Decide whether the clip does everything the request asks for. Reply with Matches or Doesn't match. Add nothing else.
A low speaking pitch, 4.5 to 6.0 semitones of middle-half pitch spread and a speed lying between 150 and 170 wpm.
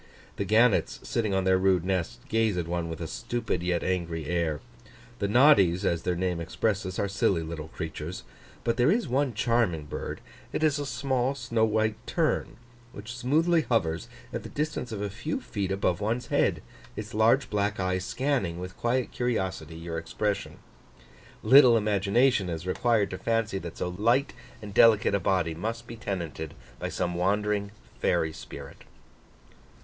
Matches